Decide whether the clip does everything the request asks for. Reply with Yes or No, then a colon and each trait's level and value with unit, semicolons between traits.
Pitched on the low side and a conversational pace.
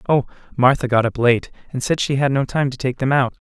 No: low, 130 Hz; fast, 260 wpm